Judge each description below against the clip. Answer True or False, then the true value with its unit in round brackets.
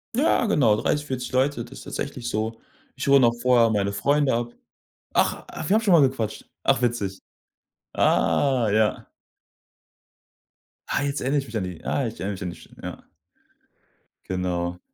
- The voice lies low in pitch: True (120 Hz)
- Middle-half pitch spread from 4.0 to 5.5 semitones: True (4.9 semitones)